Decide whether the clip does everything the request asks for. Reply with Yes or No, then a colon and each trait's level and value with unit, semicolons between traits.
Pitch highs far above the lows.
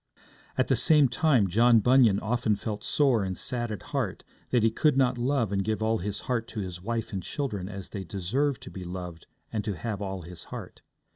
No: average, 4.2 semitones